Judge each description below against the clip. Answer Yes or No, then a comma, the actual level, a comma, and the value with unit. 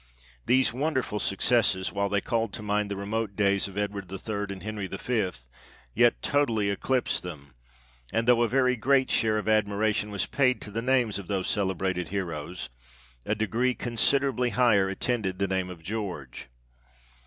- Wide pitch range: No, average, 3.6 semitones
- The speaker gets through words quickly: No, average, 175 wpm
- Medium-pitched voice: No, low, 105 Hz